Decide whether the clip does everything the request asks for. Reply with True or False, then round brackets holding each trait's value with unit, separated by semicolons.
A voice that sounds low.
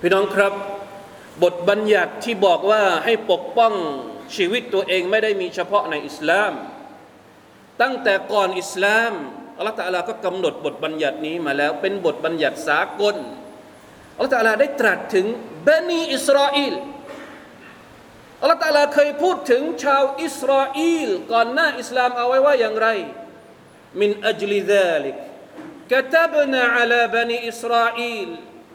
False (230 Hz)